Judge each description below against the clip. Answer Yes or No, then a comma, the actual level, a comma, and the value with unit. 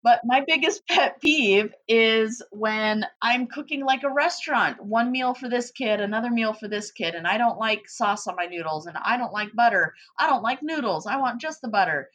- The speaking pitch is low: No, high, 235 Hz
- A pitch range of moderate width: Yes, average, 3.9 semitones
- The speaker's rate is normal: No, fast, 215 wpm